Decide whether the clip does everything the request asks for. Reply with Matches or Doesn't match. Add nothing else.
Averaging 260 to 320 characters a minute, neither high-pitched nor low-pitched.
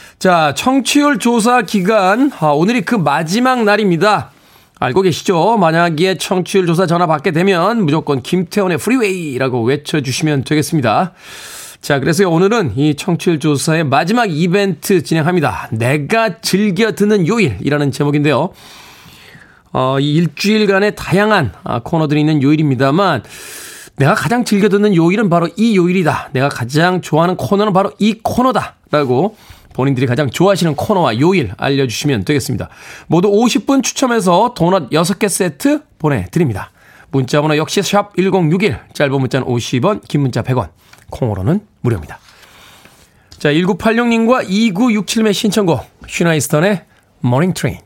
Matches